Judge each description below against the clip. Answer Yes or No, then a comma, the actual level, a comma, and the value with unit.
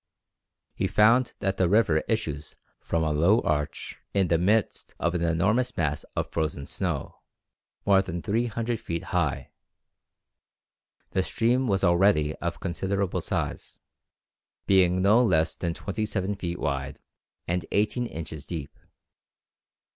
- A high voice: No, very low, 90 Hz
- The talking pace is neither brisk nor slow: No, slow, 130 wpm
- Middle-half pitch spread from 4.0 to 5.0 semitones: Yes, average, 4.3 semitones